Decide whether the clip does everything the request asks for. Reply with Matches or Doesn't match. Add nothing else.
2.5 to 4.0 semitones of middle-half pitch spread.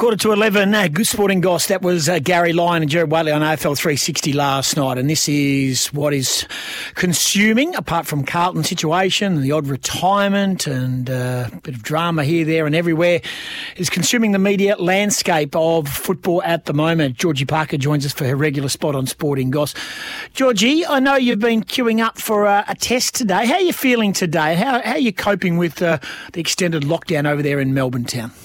Doesn't match